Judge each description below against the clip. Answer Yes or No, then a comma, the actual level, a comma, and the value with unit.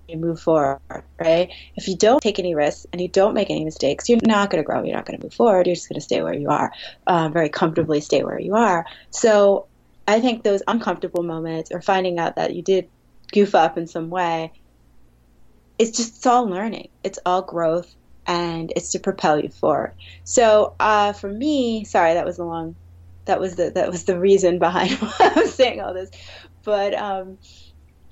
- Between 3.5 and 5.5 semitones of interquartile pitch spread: Yes, average, 3.8 semitones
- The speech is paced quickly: Yes, fast, 210 wpm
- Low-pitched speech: No, medium, 175 Hz